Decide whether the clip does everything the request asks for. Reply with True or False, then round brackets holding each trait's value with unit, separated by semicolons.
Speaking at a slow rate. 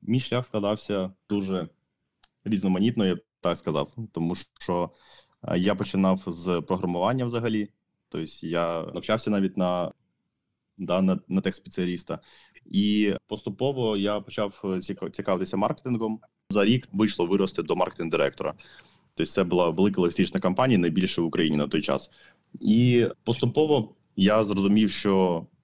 False (130 wpm)